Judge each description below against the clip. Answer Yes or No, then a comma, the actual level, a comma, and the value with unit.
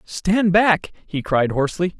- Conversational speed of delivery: Yes, average, 150 wpm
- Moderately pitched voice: Yes, medium, 175 Hz